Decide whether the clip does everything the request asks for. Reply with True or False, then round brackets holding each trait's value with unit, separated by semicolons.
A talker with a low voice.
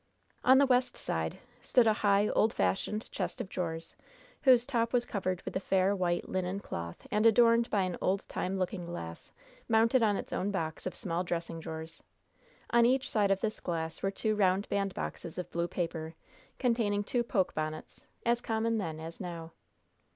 False (195 Hz)